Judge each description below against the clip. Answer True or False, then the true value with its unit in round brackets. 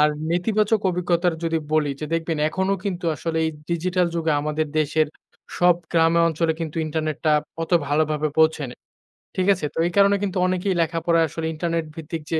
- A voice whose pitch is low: False (165 Hz)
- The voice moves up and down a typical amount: False (2.2 semitones)